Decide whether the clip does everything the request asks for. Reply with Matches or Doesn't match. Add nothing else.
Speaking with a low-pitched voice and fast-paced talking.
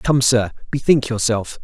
Doesn't match